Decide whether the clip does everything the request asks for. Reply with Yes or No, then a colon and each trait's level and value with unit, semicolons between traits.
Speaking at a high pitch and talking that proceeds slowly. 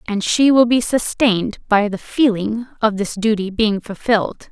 No: high, 220 Hz; average, 175 wpm